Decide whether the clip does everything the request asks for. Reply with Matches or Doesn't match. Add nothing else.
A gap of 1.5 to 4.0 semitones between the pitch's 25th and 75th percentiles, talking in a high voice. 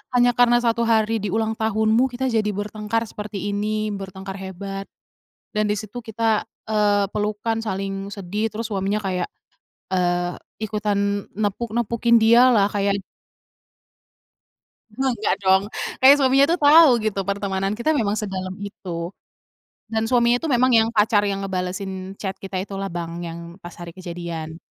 Matches